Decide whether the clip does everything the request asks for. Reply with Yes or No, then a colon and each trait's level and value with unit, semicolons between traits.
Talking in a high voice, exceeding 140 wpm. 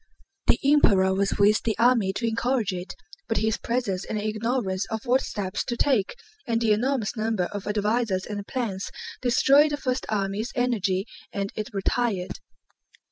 Yes: high, 215 Hz; average, 160 wpm